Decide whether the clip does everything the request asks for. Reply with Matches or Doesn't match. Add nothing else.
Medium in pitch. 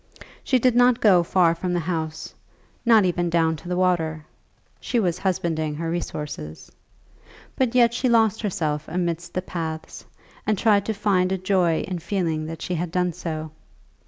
Matches